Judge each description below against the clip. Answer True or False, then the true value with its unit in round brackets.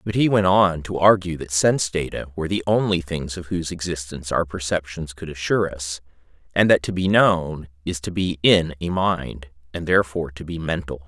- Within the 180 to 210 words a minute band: True (200 wpm)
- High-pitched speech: False (85 Hz)